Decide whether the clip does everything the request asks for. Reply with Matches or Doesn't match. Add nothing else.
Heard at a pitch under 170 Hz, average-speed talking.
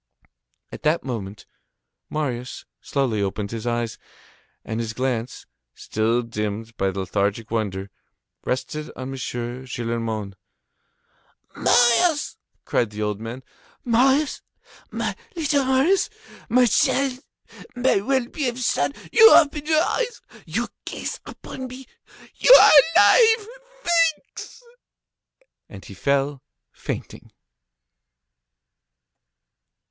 Doesn't match